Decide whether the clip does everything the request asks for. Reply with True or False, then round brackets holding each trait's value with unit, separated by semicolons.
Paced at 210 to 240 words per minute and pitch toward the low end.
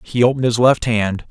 True (230 wpm; 120 Hz)